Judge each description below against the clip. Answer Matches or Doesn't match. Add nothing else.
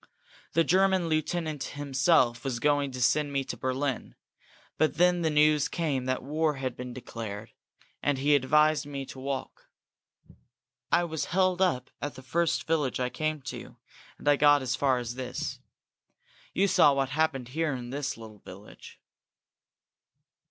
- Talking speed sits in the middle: Matches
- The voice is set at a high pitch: Doesn't match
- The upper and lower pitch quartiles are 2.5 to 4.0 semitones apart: Matches